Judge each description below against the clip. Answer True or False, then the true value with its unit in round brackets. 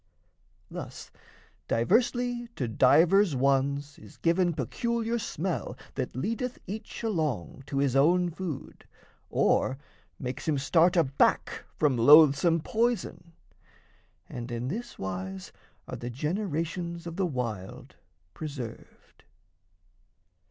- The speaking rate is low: True (105 wpm)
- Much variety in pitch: True (6.2 semitones)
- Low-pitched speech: False (155 Hz)